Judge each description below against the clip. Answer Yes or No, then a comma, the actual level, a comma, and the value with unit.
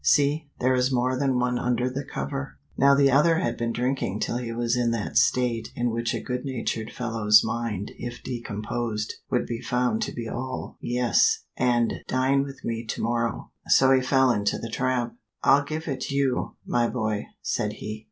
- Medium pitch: No, low, 125 Hz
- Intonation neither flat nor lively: No, narrow, 2.3 semitones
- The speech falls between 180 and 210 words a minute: Yes, average, 190 wpm